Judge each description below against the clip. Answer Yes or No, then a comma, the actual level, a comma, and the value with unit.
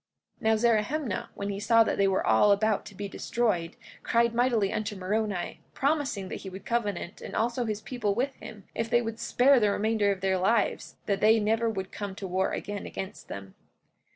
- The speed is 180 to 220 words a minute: Yes, fast, 205 wpm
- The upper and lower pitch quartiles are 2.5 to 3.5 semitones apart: Yes, average, 2.8 semitones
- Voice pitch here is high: Yes, high, 210 Hz